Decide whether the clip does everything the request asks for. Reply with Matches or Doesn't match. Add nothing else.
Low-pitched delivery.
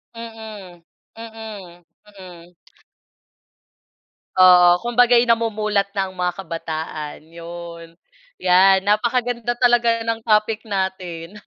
Doesn't match